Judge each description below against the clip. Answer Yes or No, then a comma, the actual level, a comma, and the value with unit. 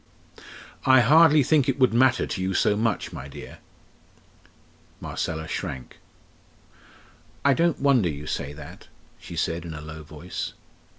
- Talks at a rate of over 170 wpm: No, average, 140 wpm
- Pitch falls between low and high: No, low, 105 Hz